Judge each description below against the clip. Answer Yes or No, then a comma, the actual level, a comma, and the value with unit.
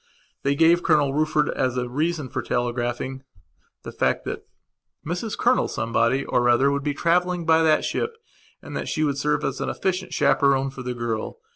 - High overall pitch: No, medium, 140 Hz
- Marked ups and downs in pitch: No, average, 4.2 semitones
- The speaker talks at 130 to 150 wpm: No, average, 180 wpm